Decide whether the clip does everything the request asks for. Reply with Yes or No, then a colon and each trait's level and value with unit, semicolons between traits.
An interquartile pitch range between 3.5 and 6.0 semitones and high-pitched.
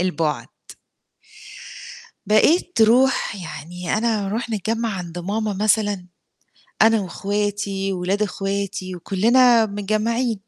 No: average, 2.7 semitones; high, 205 Hz